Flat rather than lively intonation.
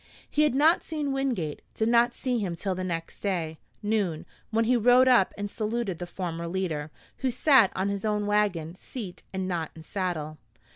No: wide, 5.5 semitones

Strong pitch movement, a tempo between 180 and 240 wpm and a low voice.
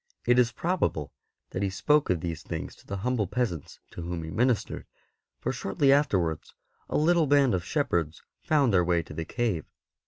Yes: wide, 8.0 semitones; average, 185 wpm; low, 100 Hz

